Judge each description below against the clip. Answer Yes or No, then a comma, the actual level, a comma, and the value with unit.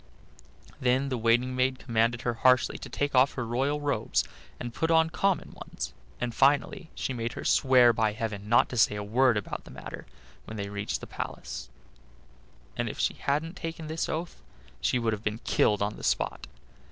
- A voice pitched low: Yes, low, 125 Hz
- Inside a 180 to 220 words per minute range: Yes, average, 200 wpm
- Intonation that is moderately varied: Yes, average, 4.1 semitones